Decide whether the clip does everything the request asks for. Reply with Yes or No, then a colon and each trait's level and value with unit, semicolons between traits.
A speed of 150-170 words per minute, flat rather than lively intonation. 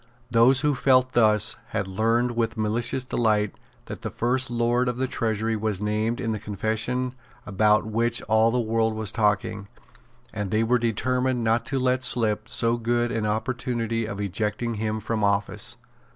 Yes: average, 165 wpm; narrow, 2.1 semitones